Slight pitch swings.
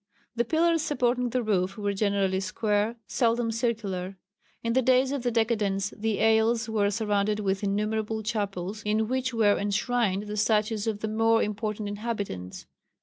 Yes: narrow, 2.2 semitones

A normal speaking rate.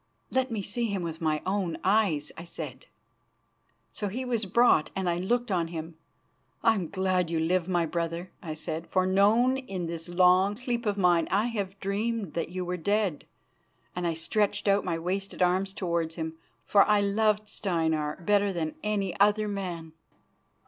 Yes: average, 175 wpm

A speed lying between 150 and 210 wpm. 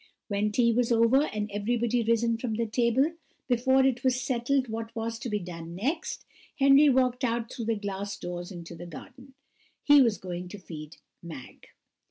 Yes: average, 180 wpm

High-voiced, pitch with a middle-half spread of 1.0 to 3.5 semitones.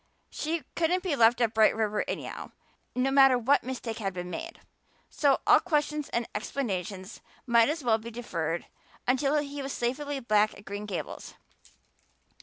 No: high, 240 Hz; average, 4.9 semitones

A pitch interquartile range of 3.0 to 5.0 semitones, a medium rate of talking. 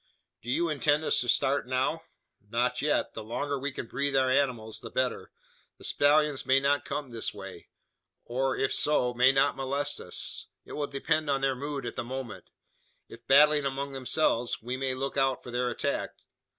No: narrow, 2.4 semitones; average, 190 wpm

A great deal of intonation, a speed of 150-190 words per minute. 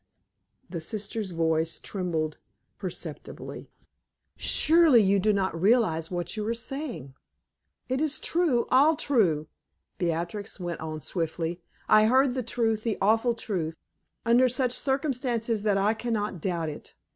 No: wide, 6.3 semitones; slow, 135 wpm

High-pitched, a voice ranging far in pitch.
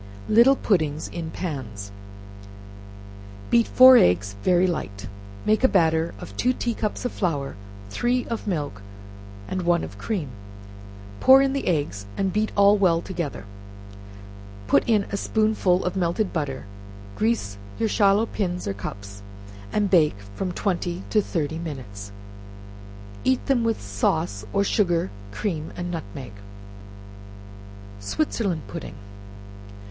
No: medium, 175 Hz; wide, 6.9 semitones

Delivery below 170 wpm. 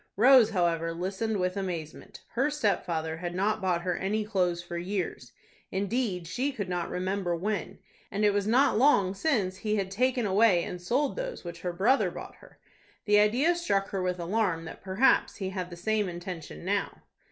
No: average, 175 wpm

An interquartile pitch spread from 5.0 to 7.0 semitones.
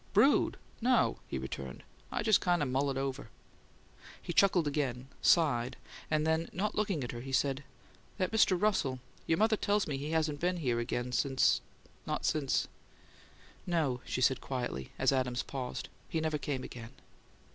Yes: wide, 5.4 semitones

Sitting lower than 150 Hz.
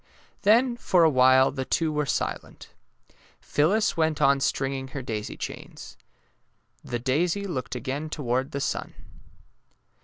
Yes: medium, 140 Hz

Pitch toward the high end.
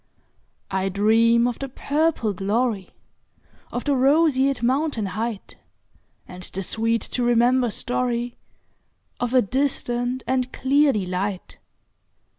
Yes: high, 240 Hz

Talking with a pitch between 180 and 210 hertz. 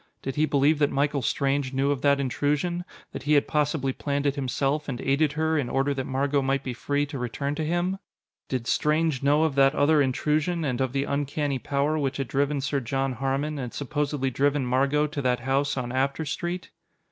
No: medium, 140 Hz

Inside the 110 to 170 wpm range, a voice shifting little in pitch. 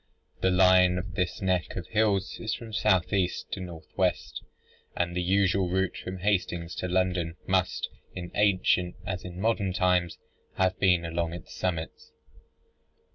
Yes: average, 155 wpm; narrow, 1.4 semitones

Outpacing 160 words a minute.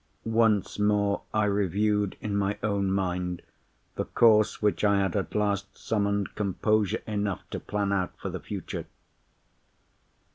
No: average, 140 wpm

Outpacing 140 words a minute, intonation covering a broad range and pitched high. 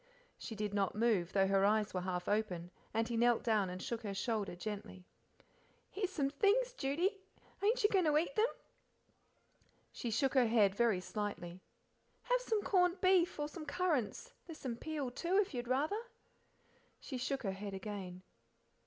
Yes: average, 170 wpm; wide, 9.0 semitones; high, 235 Hz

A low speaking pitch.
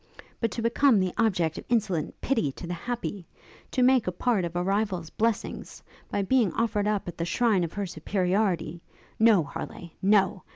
No: high, 200 Hz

